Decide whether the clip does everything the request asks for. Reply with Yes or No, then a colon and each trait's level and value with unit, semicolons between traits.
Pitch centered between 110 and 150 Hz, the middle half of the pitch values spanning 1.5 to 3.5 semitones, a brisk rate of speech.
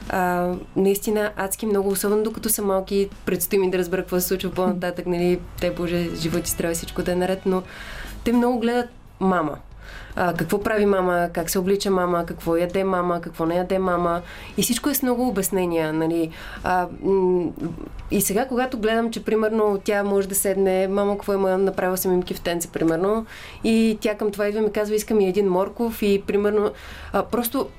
No: high, 195 Hz; average, 2.8 semitones; fast, 190 wpm